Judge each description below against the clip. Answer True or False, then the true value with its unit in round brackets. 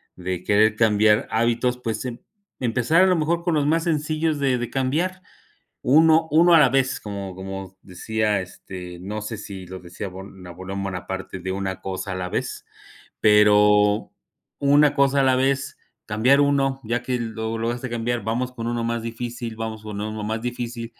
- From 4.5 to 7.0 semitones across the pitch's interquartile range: True (4.9 semitones)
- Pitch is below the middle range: True (115 Hz)